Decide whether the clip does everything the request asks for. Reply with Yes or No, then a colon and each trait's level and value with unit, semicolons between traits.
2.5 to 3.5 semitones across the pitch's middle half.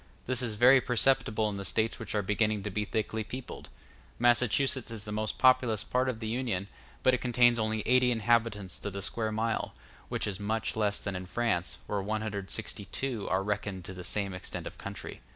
Yes: average, 2.9 semitones